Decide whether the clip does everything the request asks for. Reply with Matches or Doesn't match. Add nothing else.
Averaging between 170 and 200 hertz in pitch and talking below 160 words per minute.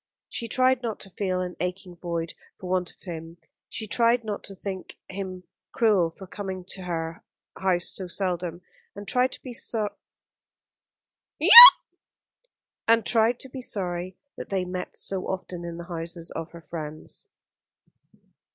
Matches